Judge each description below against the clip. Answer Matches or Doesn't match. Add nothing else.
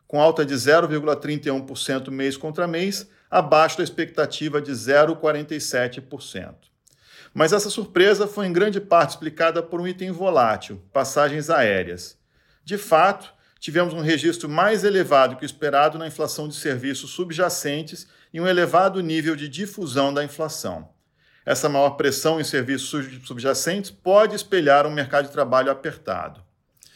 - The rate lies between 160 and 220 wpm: Doesn't match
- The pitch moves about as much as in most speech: Matches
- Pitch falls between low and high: Matches